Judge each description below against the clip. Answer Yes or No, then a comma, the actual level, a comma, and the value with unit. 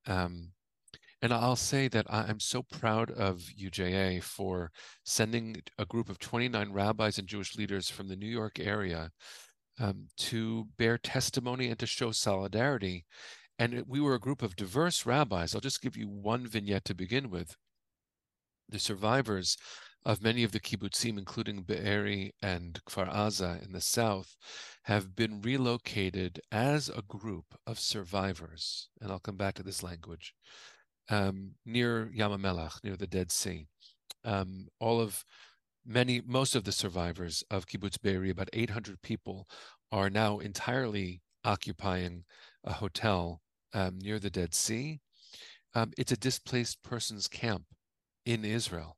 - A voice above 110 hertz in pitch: No, low, 105 Hz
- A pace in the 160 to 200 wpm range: No, average, 145 wpm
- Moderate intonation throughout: Yes, average, 3.5 semitones